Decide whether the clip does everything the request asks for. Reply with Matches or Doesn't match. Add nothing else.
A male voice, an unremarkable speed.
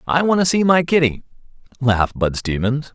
Matches